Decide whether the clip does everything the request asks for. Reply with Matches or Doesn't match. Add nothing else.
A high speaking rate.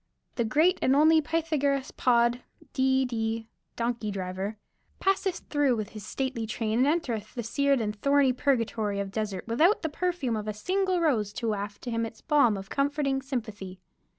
Doesn't match